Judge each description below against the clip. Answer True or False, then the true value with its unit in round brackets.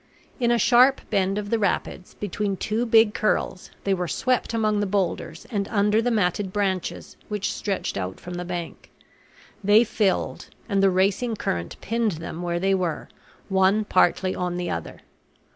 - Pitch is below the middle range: False (200 Hz)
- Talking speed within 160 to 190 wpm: True (170 wpm)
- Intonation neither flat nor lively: True (3.1 semitones)